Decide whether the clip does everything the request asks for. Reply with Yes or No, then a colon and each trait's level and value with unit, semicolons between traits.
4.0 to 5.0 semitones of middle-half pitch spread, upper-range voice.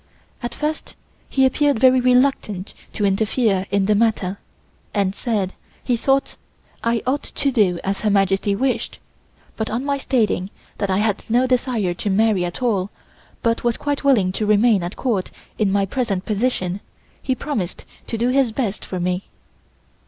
Yes: average, 4.5 semitones; high, 220 Hz